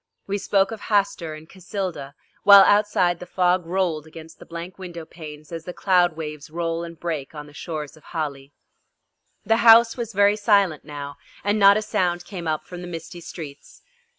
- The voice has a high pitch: No, medium, 175 Hz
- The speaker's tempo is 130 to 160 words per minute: No, average, 190 wpm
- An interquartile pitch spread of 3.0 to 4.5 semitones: Yes, average, 3.9 semitones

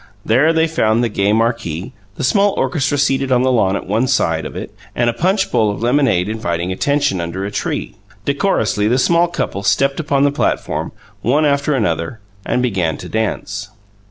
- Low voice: Yes, low, 120 Hz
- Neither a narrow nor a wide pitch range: No, wide, 6.2 semitones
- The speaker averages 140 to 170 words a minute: No, average, 185 wpm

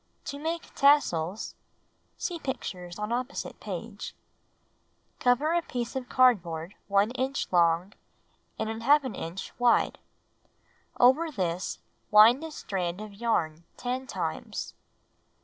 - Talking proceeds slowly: Yes, slow, 120 wpm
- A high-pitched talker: Yes, high, 235 Hz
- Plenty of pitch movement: Yes, wide, 6.3 semitones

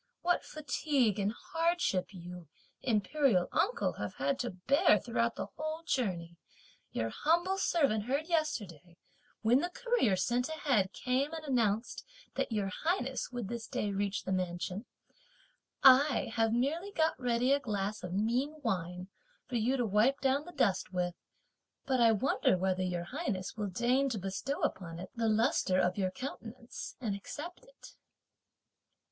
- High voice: Yes, high, 235 Hz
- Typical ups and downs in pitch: No, wide, 6.5 semitones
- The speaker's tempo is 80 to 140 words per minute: No, average, 155 wpm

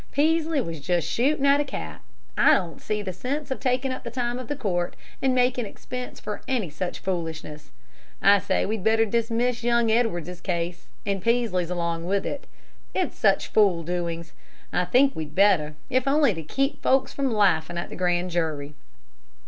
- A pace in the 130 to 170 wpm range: No, average, 180 wpm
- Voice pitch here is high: Yes, high, 205 Hz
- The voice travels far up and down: Yes, wide, 6.5 semitones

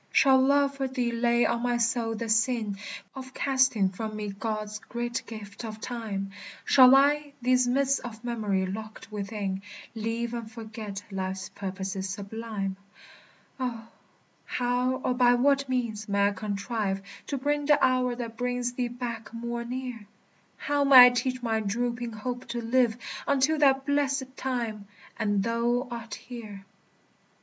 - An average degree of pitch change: Yes, average, 3.0 semitones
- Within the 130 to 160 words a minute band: Yes, average, 150 wpm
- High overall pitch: Yes, high, 235 Hz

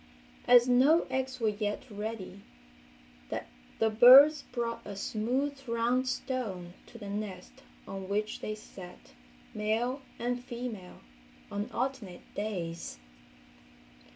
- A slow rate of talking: Yes, slow, 110 wpm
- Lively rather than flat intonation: No, average, 3.8 semitones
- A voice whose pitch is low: No, high, 220 Hz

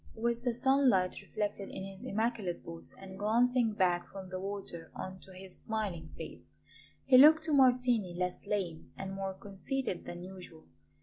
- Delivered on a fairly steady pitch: No, average, 4.4 semitones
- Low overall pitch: No, high, 195 Hz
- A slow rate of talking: No, average, 165 wpm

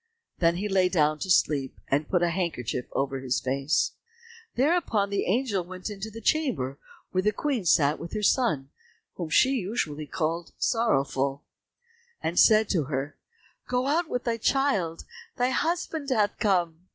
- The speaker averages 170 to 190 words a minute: No, average, 160 wpm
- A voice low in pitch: No, medium, 185 Hz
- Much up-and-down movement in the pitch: Yes, wide, 7.1 semitones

